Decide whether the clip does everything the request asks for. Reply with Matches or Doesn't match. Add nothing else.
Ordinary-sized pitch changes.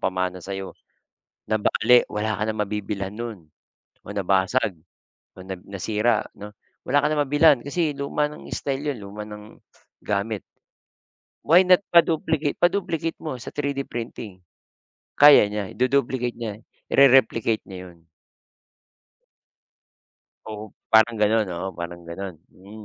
Doesn't match